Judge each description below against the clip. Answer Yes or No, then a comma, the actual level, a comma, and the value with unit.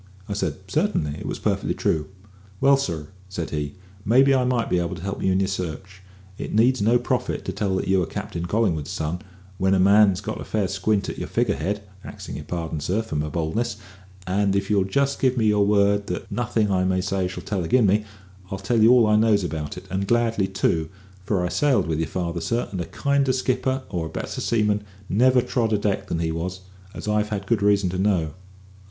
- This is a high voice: No, low, 100 Hz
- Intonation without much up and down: No, average, 3.6 semitones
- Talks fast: Yes, fast, 225 wpm